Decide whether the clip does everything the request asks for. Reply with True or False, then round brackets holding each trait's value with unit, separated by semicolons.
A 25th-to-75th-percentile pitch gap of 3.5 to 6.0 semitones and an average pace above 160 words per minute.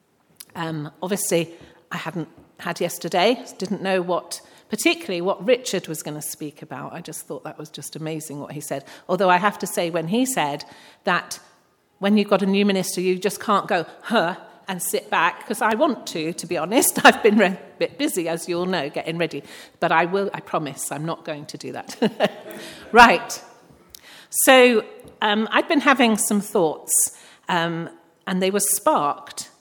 True (4.7 semitones; 190 wpm)